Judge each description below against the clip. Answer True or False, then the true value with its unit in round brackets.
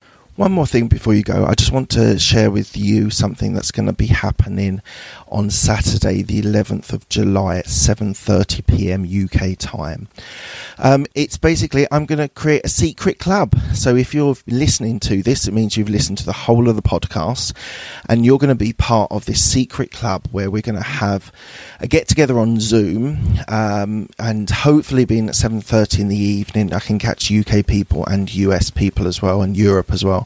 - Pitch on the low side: True (105 Hz)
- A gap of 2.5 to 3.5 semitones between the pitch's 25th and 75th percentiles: True (2.8 semitones)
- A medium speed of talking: True (190 wpm)